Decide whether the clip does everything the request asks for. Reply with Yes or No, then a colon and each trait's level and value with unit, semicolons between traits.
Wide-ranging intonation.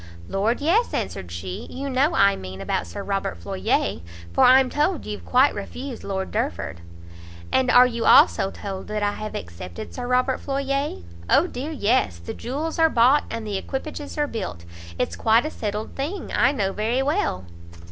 Yes: wide, 6.1 semitones